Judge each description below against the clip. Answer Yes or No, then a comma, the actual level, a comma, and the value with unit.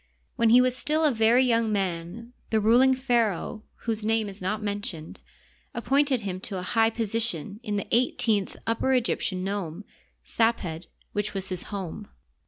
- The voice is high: Yes, high, 220 Hz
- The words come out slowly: No, average, 160 wpm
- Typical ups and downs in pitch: Yes, average, 3.3 semitones